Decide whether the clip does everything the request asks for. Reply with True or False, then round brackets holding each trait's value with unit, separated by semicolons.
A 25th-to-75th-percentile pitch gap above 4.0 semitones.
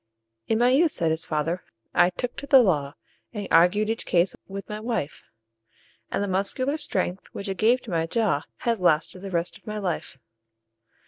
True (4.9 semitones)